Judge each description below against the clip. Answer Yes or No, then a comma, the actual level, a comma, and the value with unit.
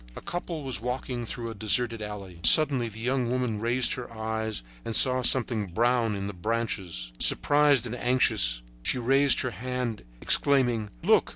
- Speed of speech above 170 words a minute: No, average, 165 wpm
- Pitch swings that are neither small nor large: Yes, average, 3.0 semitones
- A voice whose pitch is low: Yes, low, 120 Hz